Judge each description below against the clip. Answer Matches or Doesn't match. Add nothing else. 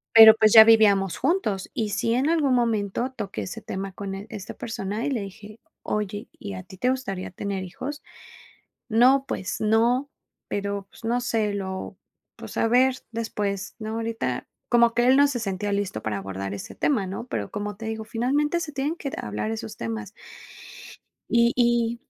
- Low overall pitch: Doesn't match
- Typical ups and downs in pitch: Matches